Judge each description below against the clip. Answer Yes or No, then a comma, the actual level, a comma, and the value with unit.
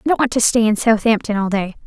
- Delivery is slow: No, fast, 290 wpm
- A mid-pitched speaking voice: No, high, 220 Hz